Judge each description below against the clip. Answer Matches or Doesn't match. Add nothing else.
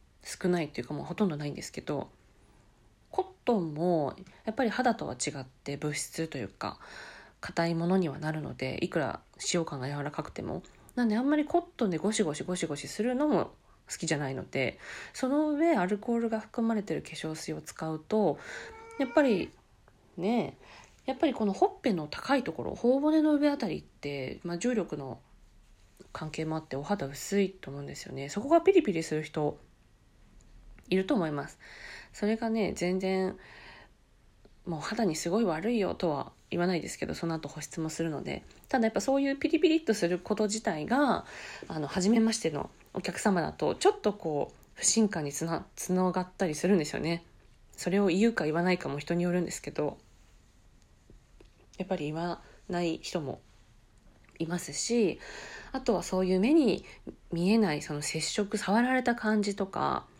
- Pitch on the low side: Doesn't match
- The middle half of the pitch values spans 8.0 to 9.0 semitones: Doesn't match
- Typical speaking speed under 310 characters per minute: Doesn't match